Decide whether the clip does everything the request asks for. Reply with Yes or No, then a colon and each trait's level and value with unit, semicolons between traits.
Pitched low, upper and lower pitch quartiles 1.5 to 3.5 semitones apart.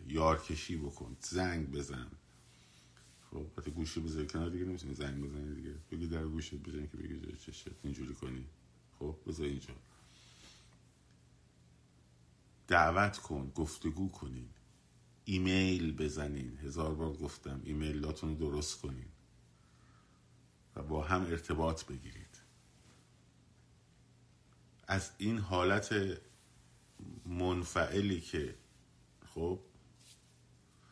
No: very low, 75 Hz; average, 4.2 semitones